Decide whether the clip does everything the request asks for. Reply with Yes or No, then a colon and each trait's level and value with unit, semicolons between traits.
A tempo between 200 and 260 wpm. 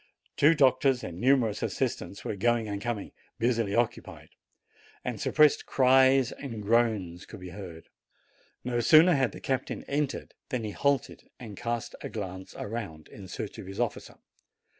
No: average, 155 wpm